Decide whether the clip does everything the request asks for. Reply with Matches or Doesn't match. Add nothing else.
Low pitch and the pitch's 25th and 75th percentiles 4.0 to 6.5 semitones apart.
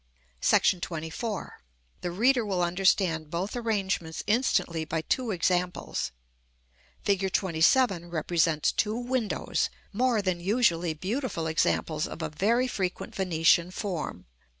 Doesn't match